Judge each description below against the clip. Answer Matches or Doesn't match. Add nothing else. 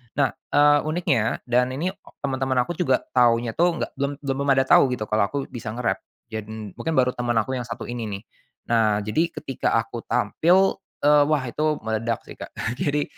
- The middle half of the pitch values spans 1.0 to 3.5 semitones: Doesn't match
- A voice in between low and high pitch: Doesn't match